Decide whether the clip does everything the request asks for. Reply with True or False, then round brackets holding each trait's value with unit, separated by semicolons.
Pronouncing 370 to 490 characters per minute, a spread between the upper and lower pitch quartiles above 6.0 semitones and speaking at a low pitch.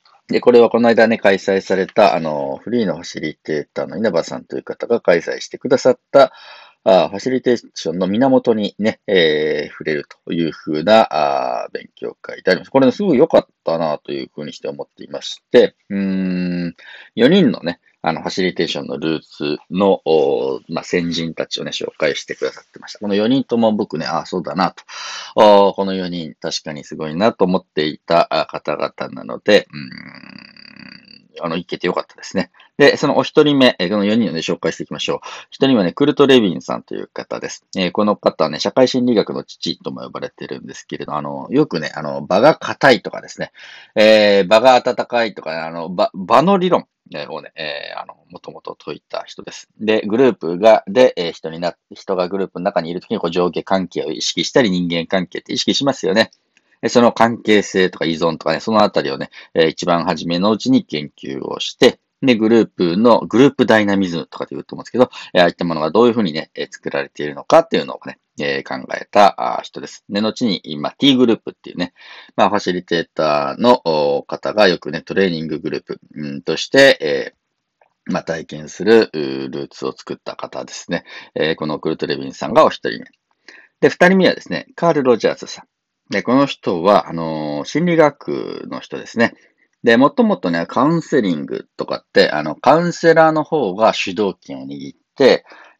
True (380 characters per minute; 8.2 semitones; 105 Hz)